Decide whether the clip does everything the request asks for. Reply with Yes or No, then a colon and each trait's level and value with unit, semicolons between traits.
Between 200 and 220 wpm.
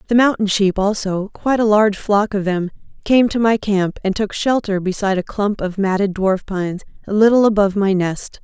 Yes: fast, 205 wpm